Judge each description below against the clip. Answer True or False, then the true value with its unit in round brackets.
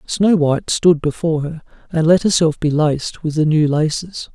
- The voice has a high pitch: False (160 Hz)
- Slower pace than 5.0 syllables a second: False (5.1 syllables/s)